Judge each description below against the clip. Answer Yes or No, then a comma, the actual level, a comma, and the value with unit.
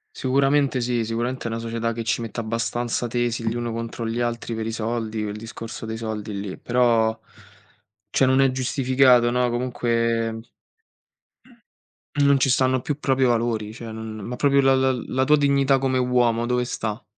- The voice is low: Yes, low, 120 Hz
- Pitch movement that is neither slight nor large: No, narrow, 2.3 semitones